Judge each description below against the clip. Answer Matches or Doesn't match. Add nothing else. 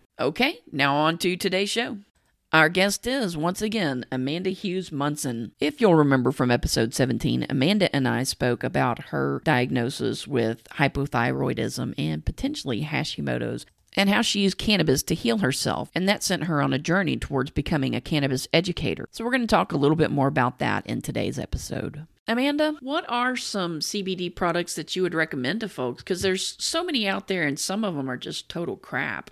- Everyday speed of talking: Matches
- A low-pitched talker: Doesn't match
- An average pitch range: Doesn't match